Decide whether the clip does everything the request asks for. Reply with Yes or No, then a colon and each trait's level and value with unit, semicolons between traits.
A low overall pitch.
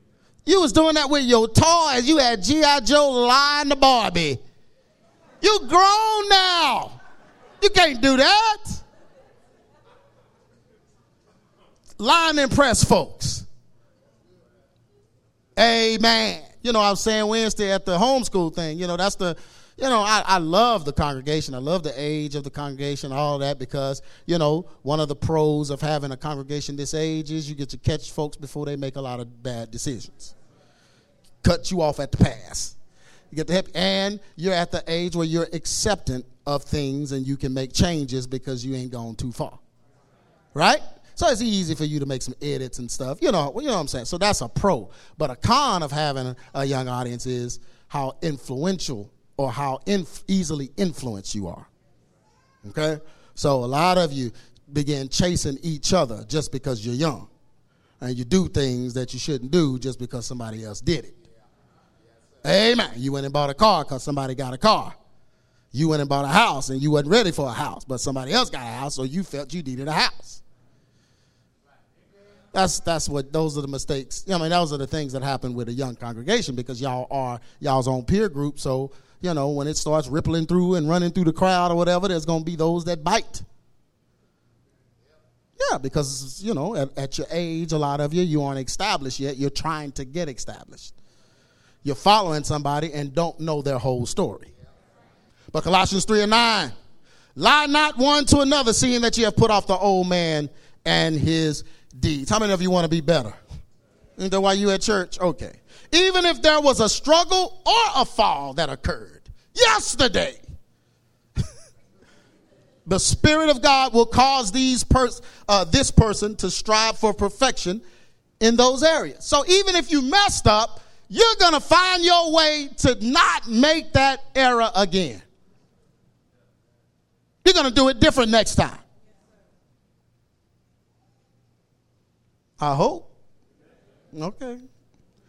No: medium, 160 Hz